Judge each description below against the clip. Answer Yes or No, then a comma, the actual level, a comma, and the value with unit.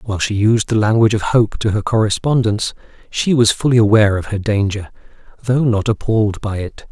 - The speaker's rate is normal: Yes, average, 190 wpm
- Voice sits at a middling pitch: No, low, 110 Hz